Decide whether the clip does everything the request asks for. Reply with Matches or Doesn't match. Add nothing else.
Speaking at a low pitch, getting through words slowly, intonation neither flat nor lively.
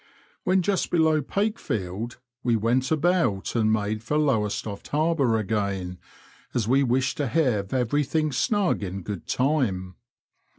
Doesn't match